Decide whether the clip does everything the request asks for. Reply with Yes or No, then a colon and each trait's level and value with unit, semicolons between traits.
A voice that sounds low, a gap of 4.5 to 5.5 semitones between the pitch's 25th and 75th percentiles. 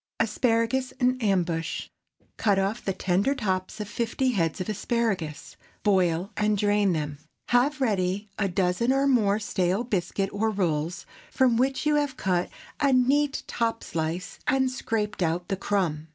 No: high, 205 Hz; average, 5.1 semitones